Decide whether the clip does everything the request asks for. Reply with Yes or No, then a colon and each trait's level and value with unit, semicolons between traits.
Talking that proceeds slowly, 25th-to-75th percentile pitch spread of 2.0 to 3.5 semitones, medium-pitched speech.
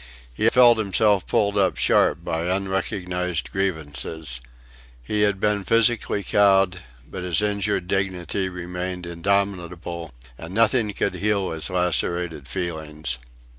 No: slow, 120 wpm; average, 2.8 semitones; very low, 90 Hz